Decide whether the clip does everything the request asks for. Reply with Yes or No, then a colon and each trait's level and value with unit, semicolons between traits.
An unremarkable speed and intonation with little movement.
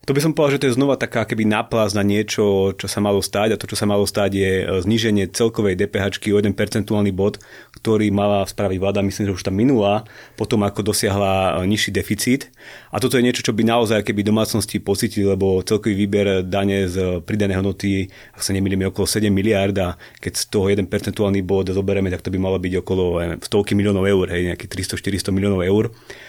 No: fast, 210 wpm; narrow, 2.0 semitones